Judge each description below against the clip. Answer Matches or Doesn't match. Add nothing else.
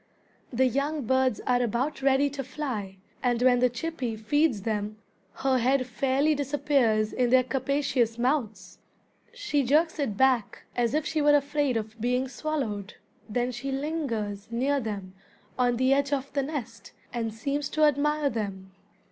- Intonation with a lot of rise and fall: Doesn't match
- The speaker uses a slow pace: Doesn't match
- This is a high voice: Matches